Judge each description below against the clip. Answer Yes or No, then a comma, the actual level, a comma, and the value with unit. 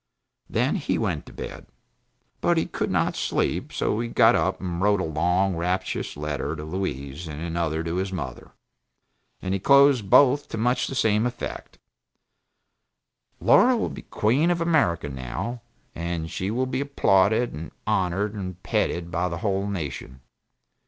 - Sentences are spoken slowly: No, average, 160 wpm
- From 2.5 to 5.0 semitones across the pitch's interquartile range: No, wide, 5.6 semitones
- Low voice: Yes, very low, 95 Hz